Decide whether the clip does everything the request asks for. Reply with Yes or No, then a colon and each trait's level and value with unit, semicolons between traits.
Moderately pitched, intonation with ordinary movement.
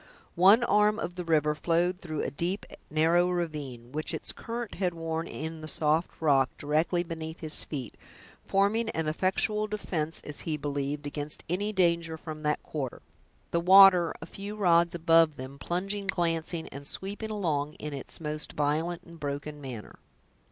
Yes: medium, 165 Hz; average, 3.2 semitones